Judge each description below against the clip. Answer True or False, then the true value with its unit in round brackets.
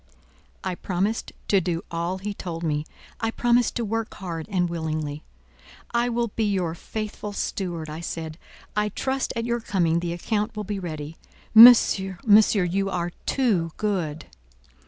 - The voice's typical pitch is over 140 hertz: True (190 Hz)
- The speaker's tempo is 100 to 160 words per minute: True (155 wpm)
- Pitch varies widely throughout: False (4.5 semitones)